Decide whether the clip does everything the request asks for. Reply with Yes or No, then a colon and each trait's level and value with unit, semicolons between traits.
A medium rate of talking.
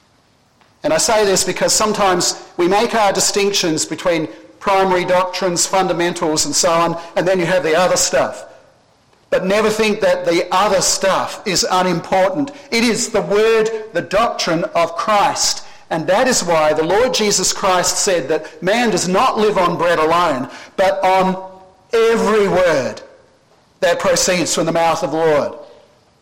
Yes: average, 160 wpm